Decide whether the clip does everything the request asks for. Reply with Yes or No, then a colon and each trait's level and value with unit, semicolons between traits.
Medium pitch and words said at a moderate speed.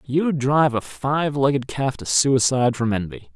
No: low, 130 Hz; average, 180 wpm